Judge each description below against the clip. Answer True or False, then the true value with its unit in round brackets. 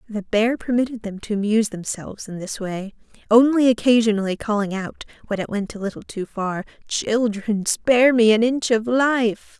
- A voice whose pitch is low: False (220 Hz)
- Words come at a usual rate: True (175 wpm)